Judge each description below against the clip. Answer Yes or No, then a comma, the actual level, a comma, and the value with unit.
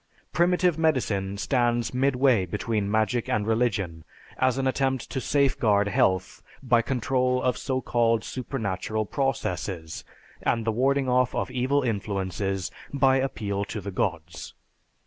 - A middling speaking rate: No, slow, 130 wpm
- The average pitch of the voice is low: Yes, low, 120 Hz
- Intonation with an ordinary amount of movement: Yes, average, 4.6 semitones